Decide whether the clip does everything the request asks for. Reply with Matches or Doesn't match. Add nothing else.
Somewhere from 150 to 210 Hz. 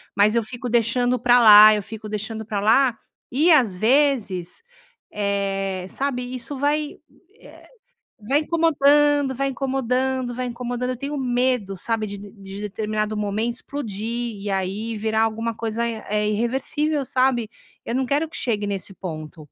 Doesn't match